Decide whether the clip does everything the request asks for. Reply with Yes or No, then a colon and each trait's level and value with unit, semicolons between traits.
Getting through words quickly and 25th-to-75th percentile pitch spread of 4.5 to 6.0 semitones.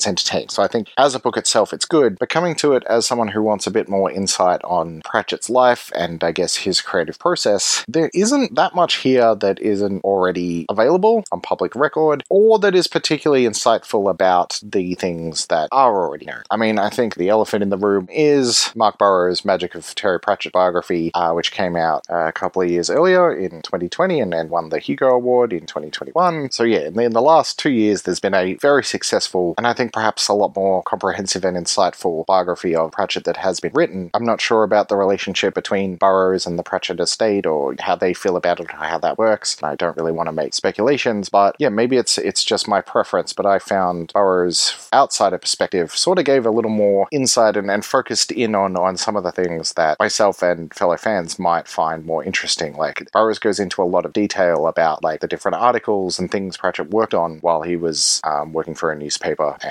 Yes: fast, 220 wpm; average, 5.2 semitones